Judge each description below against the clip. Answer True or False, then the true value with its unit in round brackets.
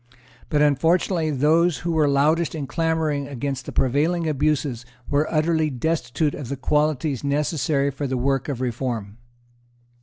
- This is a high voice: False (145 Hz)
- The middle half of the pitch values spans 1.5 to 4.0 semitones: True (2.8 semitones)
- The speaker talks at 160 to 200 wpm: False (145 wpm)